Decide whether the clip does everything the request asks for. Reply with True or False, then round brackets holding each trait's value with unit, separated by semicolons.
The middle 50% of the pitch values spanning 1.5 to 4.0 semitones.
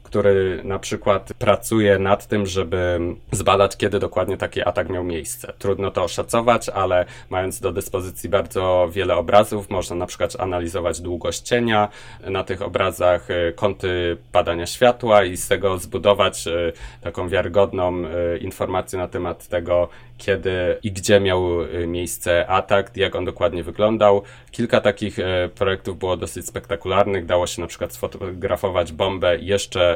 True (2.8 semitones)